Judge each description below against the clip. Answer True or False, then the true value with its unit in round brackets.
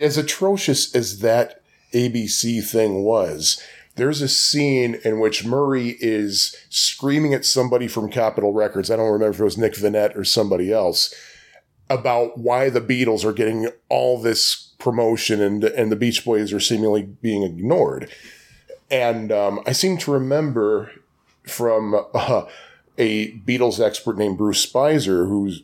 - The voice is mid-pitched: False (115 Hz)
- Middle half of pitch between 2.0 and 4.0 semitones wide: True (3.5 semitones)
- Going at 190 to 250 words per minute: False (150 wpm)